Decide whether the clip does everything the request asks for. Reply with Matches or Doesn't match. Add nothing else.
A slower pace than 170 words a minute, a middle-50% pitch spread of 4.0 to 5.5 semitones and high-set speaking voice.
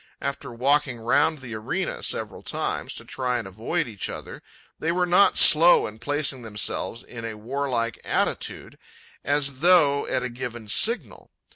Doesn't match